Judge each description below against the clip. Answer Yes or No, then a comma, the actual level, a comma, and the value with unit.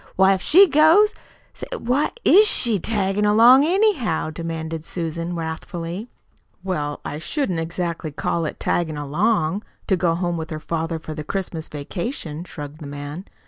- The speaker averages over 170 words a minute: No, average, 155 wpm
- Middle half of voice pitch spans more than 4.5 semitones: Yes, average, 5.0 semitones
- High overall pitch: No, medium, 170 Hz